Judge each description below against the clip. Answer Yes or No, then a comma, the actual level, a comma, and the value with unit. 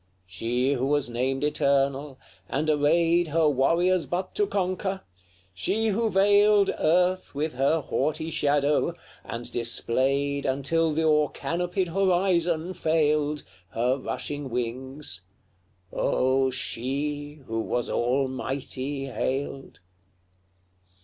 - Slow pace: Yes, slow, 105 wpm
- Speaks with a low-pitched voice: No, medium, 145 Hz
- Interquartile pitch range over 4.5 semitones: No, average, 4.2 semitones